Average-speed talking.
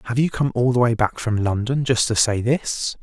No: fast, 260 wpm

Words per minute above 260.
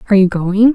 No: fast, 240 wpm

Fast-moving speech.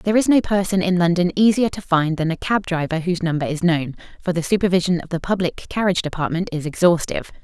Yes: fast, 220 wpm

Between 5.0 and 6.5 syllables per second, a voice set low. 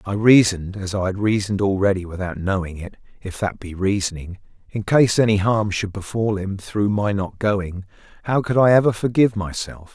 Yes: 5.4 syllables/s; low, 100 Hz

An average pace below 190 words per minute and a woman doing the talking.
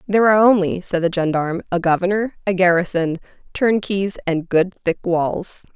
Yes: average, 155 wpm; female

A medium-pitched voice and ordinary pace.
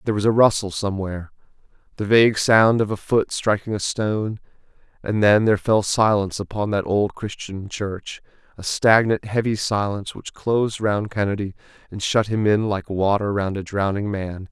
No: low, 105 Hz; average, 170 wpm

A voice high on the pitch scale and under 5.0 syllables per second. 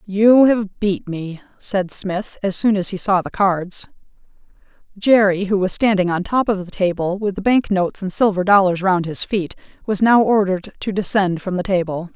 Yes: high, 195 Hz; 4.8 syllables/s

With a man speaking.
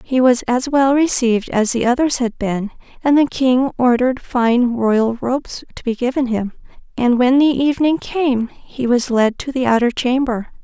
No: female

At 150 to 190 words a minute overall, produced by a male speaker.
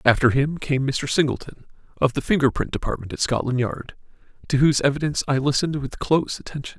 Yes: average, 185 wpm; male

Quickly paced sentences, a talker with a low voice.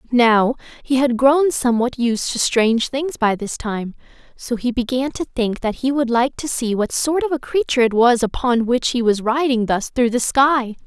No: fast, 215 wpm; high, 245 Hz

